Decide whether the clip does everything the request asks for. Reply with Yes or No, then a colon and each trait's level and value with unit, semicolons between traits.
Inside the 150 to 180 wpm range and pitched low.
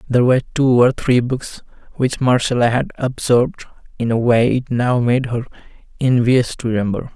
Yes: average, 170 wpm; low, 120 Hz